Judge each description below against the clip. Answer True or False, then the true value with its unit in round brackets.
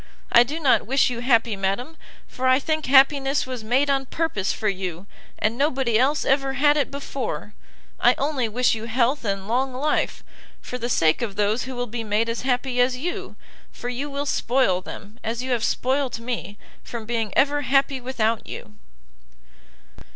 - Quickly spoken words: False (180 wpm)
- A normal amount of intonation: True (3.4 semitones)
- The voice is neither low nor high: False (250 Hz)